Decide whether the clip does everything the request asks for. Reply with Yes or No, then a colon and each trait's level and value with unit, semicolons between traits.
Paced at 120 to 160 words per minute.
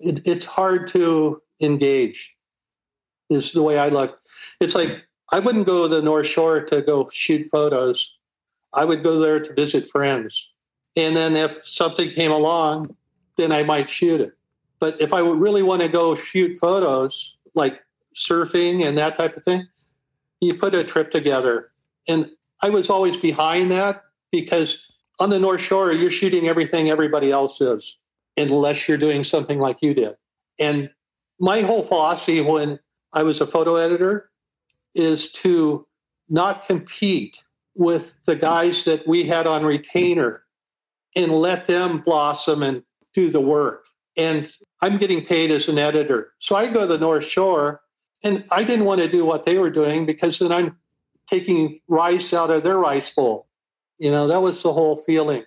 No: average, 170 wpm